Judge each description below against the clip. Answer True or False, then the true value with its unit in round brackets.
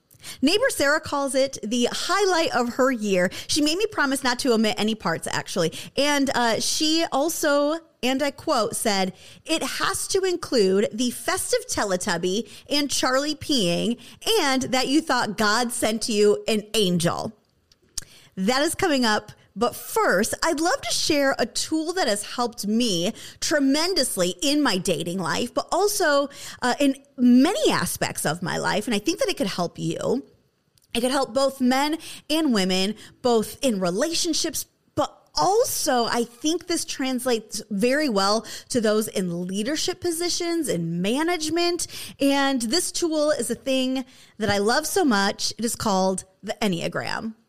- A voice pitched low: False (260 Hz)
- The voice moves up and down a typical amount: False (6.3 semitones)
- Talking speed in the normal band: True (160 wpm)